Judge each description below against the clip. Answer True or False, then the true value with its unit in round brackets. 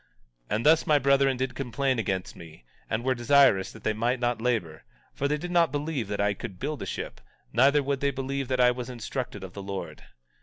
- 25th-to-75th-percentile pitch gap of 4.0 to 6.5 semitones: True (4.6 semitones)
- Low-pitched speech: True (125 Hz)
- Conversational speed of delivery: False (225 wpm)